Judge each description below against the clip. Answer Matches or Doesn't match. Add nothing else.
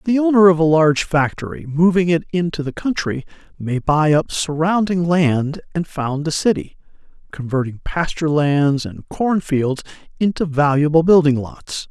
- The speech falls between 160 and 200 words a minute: Doesn't match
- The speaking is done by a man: Matches